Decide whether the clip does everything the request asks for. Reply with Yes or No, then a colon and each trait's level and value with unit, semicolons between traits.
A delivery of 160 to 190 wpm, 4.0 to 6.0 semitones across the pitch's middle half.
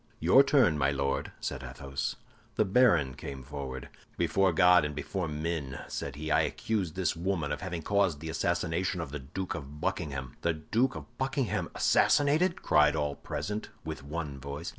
Yes: average, 170 wpm; average, 5.0 semitones